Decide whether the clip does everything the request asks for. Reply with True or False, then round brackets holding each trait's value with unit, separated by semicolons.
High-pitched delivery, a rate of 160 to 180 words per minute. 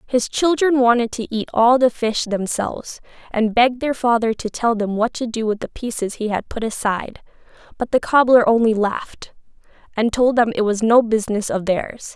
False (230 Hz; 195 wpm)